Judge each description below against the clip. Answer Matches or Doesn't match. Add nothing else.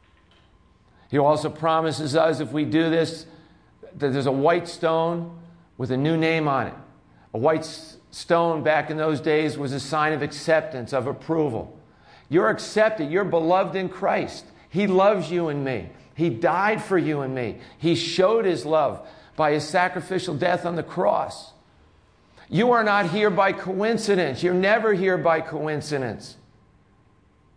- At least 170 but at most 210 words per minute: Doesn't match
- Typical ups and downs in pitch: Matches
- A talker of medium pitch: Matches